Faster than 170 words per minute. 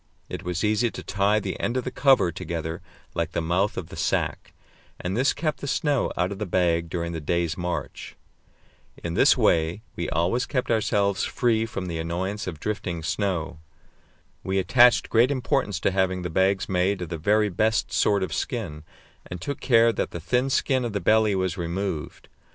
Yes: average, 190 wpm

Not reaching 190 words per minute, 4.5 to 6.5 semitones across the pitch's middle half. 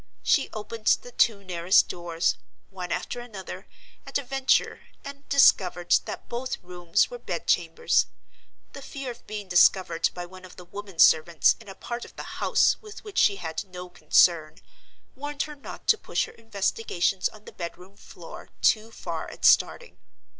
Yes: average, 170 wpm; wide, 5.6 semitones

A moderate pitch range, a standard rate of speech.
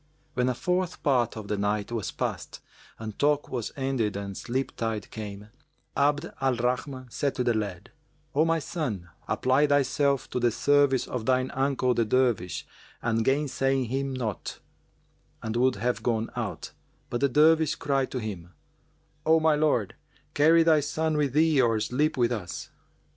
Yes: average, 4.2 semitones; average, 165 wpm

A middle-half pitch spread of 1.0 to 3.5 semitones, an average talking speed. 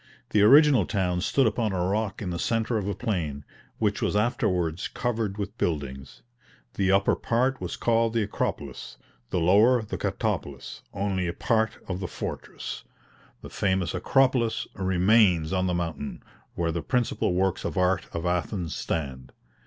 No: average, 4.2 semitones; average, 160 wpm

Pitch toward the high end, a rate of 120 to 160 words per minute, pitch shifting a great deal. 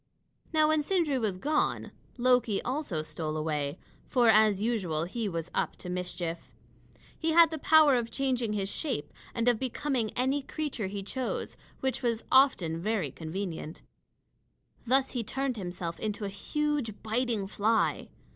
Yes: high, 225 Hz; average, 150 wpm; wide, 6.2 semitones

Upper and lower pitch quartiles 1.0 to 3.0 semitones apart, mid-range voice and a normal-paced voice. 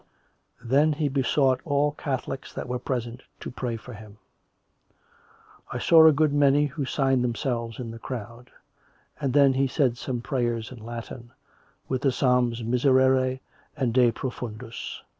No: narrow, 2.6 semitones; low, 130 Hz; average, 150 wpm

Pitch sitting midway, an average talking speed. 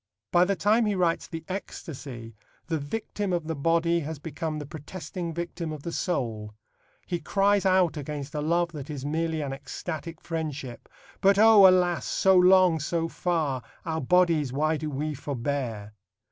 Yes: medium, 160 Hz; average, 165 wpm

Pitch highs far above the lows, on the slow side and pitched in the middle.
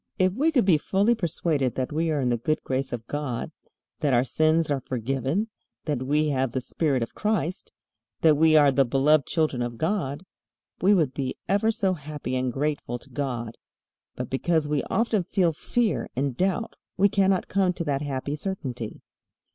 No: wide, 5.7 semitones; average, 185 wpm; medium, 150 Hz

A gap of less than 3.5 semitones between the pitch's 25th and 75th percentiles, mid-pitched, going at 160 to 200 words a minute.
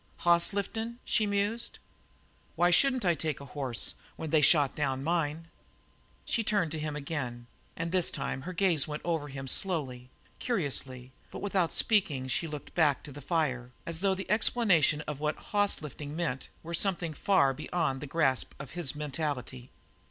No: average, 4.4 semitones; medium, 155 Hz; average, 170 wpm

